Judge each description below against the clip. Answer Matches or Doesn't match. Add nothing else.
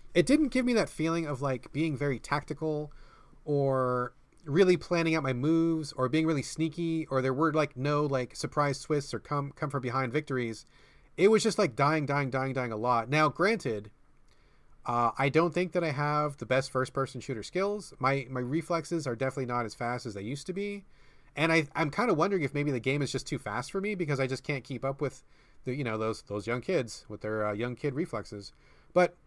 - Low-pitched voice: Doesn't match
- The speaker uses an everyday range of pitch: Matches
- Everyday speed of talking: Doesn't match